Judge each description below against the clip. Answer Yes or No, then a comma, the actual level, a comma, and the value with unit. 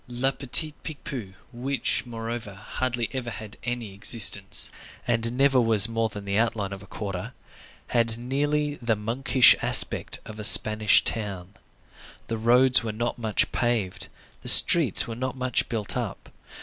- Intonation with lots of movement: No, average, 3.0 semitones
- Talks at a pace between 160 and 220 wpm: No, average, 150 wpm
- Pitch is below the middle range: Yes, low, 115 Hz